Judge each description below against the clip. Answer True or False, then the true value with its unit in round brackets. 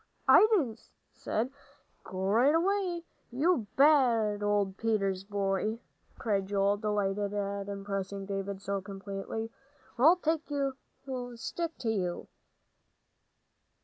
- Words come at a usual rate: False (115 wpm)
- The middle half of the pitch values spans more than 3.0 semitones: True (5.3 semitones)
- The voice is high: True (205 Hz)